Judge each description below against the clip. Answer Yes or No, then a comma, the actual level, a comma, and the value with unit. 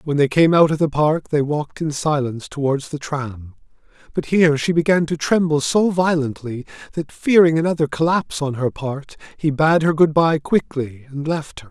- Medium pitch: Yes, medium, 150 Hz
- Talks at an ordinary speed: Yes, average, 195 wpm